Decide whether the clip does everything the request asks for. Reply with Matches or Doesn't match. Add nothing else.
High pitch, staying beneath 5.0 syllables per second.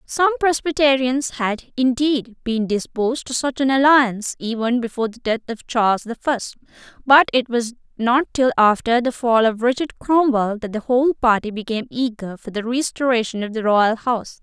Doesn't match